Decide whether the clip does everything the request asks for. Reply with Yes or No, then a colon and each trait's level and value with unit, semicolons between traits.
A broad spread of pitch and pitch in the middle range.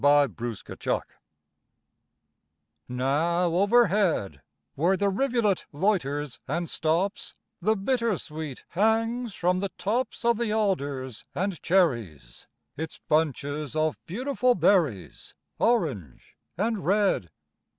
Yes: wide, 6.6 semitones; medium, 175 Hz